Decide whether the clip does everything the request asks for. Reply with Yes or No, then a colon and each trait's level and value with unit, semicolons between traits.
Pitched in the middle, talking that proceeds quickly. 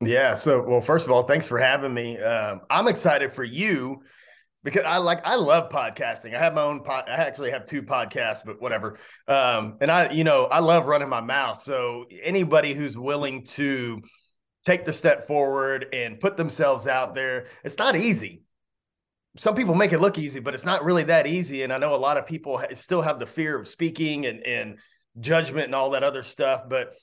Yes: medium, 145 Hz; fast, 210 wpm